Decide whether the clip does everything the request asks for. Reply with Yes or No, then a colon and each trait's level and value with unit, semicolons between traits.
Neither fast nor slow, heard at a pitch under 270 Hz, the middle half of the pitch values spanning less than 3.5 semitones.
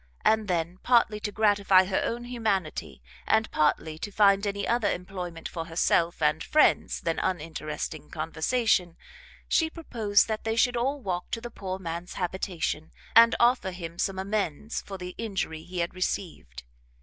No: average, 160 wpm; high, 190 Hz; average, 4.6 semitones